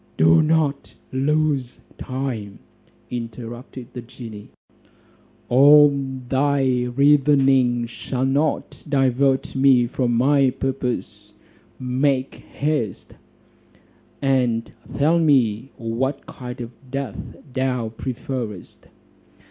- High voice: No, low, 130 Hz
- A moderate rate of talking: No, slow, 85 wpm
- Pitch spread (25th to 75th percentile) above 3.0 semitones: No, narrow, 2.6 semitones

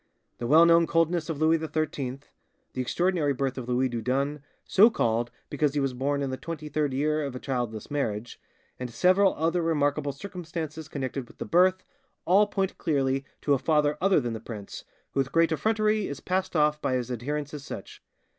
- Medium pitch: Yes, medium, 145 Hz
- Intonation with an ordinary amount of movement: Yes, average, 4.0 semitones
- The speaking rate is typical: Yes, average, 195 wpm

